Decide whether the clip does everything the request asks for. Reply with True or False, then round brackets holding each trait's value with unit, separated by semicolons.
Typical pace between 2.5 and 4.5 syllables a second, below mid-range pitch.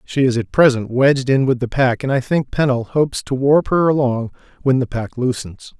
False (5.2 syllables/s; 130 Hz)